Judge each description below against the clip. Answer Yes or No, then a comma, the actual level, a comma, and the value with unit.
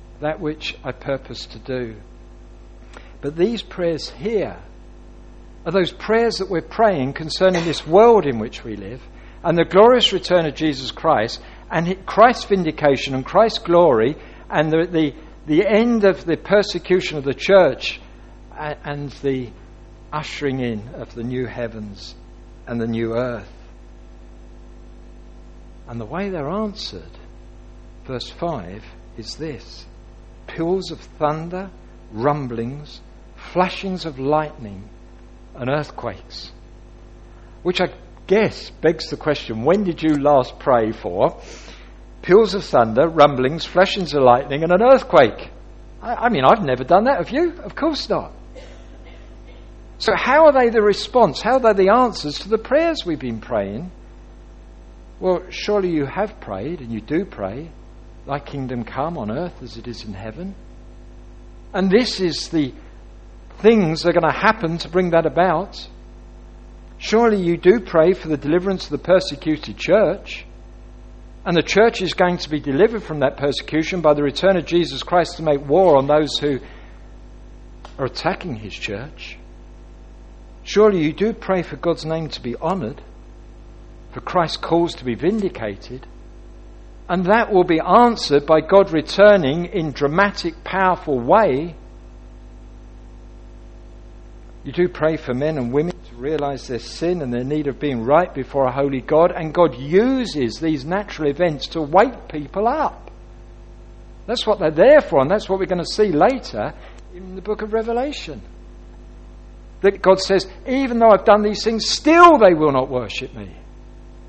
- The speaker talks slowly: No, average, 155 wpm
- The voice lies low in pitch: No, medium, 150 Hz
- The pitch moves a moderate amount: No, wide, 7.9 semitones